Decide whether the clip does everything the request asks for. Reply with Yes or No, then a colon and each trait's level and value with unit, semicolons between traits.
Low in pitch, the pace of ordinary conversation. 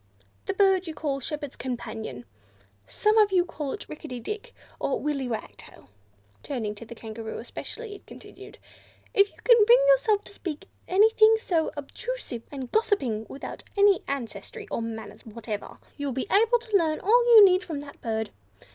No: very high, 310 Hz; average, 175 wpm